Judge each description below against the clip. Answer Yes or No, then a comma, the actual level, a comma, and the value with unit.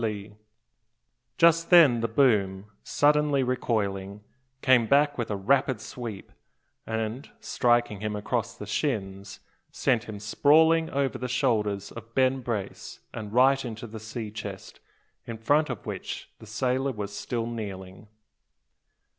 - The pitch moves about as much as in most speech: Yes, average, 4.2 semitones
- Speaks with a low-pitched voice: Yes, low, 115 Hz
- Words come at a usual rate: No, slow, 130 wpm